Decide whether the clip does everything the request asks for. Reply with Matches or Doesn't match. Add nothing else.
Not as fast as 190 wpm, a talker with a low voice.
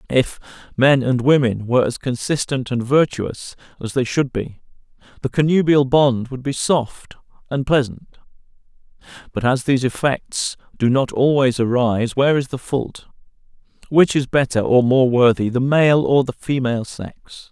Matches